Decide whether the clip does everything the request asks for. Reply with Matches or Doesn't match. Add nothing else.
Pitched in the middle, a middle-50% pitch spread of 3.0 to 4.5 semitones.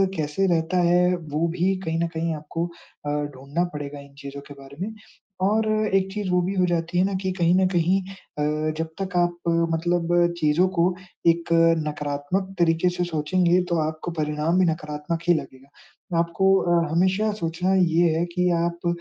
Doesn't match